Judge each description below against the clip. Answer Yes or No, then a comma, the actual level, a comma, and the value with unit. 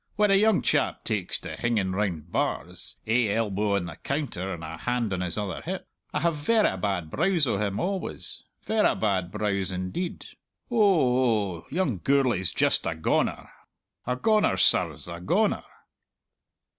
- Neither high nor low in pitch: No, low, 110 Hz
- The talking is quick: No, average, 160 wpm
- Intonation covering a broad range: Yes, wide, 8.4 semitones